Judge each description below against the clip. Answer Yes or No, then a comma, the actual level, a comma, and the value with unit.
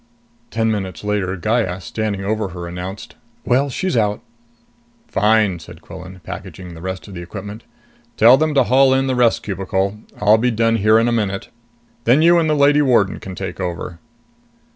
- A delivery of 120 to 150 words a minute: No, average, 180 wpm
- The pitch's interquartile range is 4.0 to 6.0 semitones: Yes, average, 4.3 semitones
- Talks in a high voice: No, low, 105 Hz